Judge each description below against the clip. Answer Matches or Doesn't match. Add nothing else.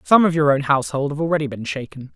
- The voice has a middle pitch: Matches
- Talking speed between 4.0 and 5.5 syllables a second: Doesn't match